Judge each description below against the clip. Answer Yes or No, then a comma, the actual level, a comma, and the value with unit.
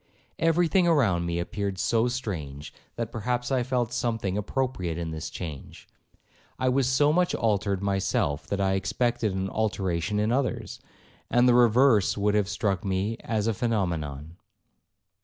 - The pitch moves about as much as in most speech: Yes, average, 4.6 semitones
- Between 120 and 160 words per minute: Yes, average, 150 wpm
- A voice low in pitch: Yes, low, 105 Hz